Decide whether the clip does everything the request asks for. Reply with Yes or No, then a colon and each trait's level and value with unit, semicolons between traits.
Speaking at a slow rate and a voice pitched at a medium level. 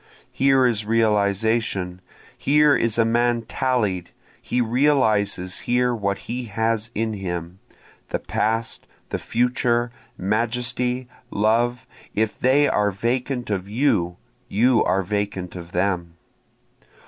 No: slow, 115 wpm; low, 110 Hz